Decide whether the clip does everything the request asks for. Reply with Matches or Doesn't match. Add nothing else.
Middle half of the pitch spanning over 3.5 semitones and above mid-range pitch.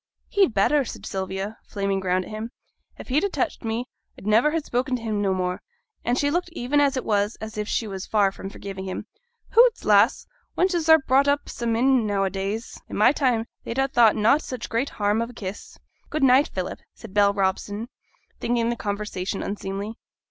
Matches